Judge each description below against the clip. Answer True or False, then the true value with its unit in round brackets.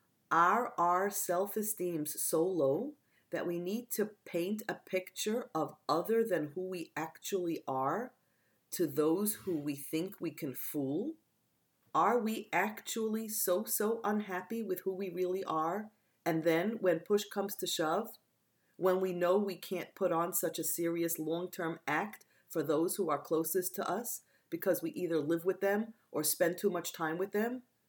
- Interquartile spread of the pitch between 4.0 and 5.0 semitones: False (3.5 semitones)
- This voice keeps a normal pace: True (170 wpm)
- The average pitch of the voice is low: False (180 Hz)